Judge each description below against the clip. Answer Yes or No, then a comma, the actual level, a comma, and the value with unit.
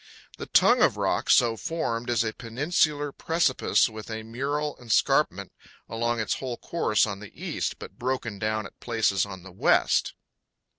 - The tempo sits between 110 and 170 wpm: Yes, average, 160 wpm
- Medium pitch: No, low, 115 Hz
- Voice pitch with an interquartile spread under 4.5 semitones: Yes, average, 4.0 semitones